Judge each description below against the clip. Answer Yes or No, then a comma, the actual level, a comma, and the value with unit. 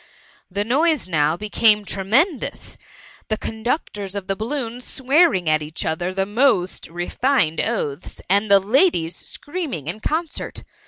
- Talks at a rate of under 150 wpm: Yes, average, 140 wpm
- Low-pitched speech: No, high, 210 Hz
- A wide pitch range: Yes, wide, 6.6 semitones